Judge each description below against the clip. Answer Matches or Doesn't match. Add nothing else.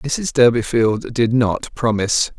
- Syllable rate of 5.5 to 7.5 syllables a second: Doesn't match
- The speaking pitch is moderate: Doesn't match